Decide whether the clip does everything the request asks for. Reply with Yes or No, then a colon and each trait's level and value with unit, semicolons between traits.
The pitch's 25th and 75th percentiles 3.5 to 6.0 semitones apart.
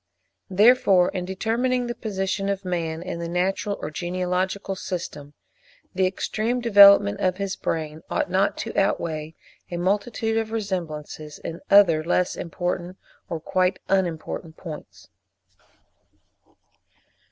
No: average, 2.9 semitones